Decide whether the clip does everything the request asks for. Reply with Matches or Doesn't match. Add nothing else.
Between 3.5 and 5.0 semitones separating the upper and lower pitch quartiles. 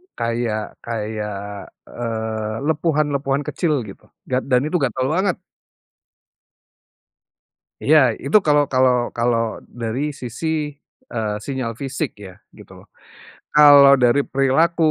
Matches